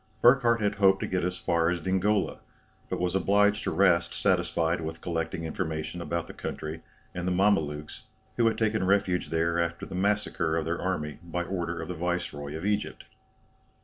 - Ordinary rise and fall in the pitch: Yes, average, 3.0 semitones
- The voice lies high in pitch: No, very low, 90 Hz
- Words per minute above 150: Yes, average, 185 wpm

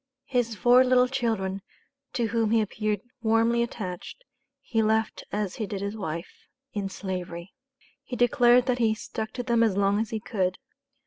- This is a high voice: Yes, high, 220 Hz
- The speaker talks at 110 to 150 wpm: No, average, 170 wpm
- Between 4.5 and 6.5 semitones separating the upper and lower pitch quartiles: No, average, 3.2 semitones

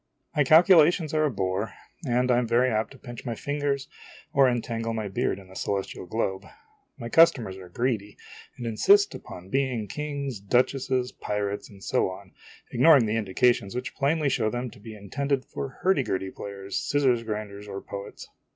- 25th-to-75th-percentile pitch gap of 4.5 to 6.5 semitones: Yes, average, 5.2 semitones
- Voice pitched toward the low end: Yes, low, 120 Hz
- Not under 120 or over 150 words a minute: No, average, 175 wpm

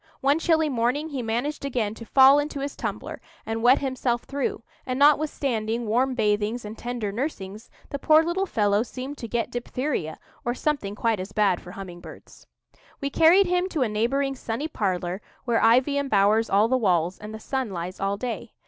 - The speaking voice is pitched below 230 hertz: No, high, 240 Hz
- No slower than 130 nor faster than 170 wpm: No, average, 185 wpm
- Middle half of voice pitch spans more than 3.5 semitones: Yes, average, 4.9 semitones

